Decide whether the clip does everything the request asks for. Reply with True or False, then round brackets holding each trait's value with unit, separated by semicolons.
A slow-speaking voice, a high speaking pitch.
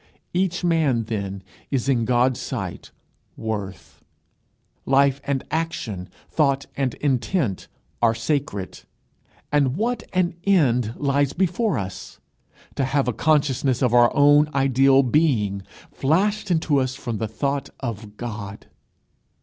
False (125 wpm; 135 Hz)